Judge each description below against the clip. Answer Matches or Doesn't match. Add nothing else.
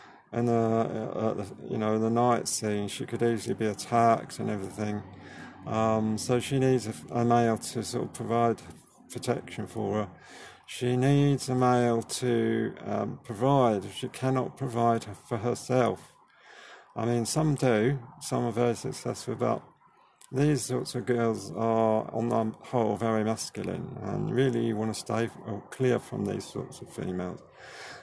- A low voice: Matches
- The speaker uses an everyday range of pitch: Doesn't match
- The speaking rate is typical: Matches